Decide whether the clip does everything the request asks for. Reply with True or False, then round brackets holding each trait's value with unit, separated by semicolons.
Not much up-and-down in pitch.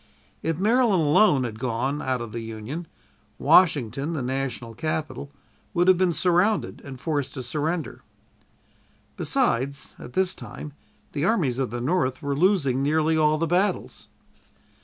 False (5.0 semitones)